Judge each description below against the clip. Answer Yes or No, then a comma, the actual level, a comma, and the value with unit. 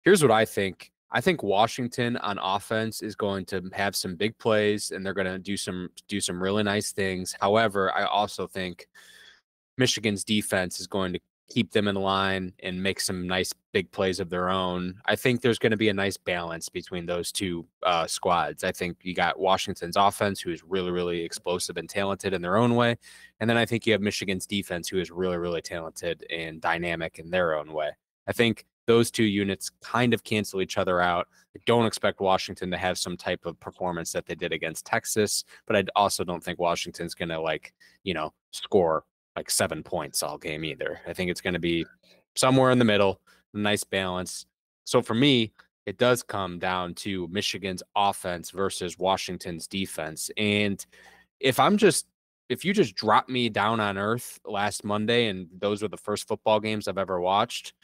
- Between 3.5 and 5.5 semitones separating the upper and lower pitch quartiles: No, average, 2.9 semitones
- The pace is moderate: Yes, average, 195 wpm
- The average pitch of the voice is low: Yes, low, 100 Hz